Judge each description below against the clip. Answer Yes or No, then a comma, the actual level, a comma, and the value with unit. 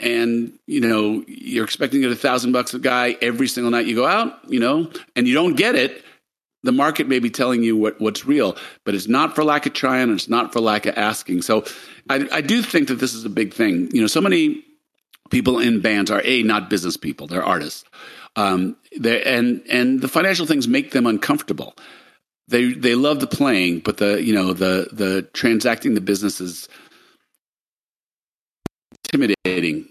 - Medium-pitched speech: No, low, 125 Hz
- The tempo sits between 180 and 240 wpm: Yes, average, 195 wpm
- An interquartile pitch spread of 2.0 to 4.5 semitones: No, average, 5.1 semitones